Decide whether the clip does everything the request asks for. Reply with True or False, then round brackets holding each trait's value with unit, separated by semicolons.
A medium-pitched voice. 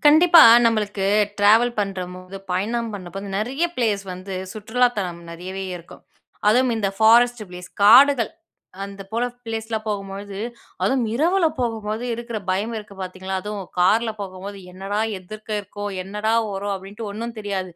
False (205 Hz)